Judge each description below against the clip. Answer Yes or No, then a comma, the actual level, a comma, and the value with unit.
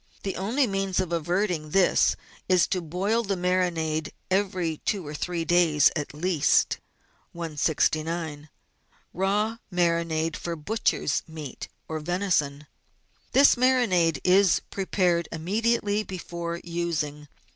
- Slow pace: Yes, slow, 115 wpm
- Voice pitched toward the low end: No, medium, 175 Hz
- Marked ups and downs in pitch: No, average, 3.4 semitones